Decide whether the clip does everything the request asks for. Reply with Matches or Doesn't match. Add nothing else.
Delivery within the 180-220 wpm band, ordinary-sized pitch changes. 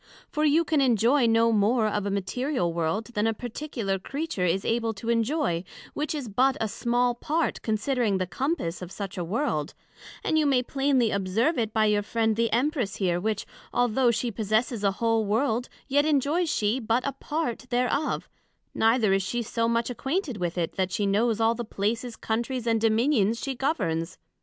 Matches